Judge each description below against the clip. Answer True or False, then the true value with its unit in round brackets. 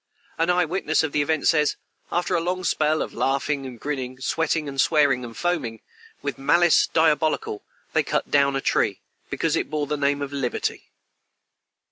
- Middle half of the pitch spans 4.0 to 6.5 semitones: False (2.9 semitones)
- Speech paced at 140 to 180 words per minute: True (170 wpm)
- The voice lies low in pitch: False (150 Hz)